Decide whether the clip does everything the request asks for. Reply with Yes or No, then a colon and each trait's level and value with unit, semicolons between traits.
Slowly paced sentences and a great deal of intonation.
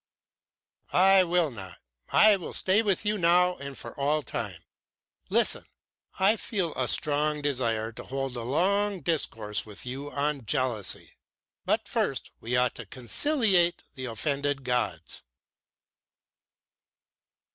Yes: slow, 125 wpm; wide, 6.5 semitones